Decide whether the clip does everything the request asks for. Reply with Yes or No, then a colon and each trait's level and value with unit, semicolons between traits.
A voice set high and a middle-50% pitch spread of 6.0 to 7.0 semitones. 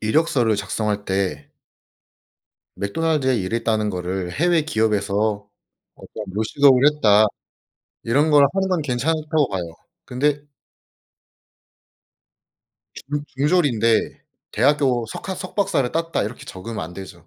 No: low, 120 Hz; wide, 6.3 semitones